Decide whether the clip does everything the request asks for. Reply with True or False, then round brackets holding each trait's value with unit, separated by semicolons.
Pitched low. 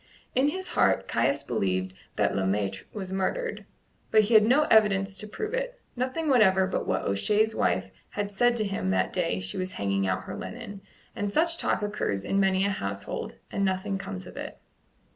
False (195 Hz)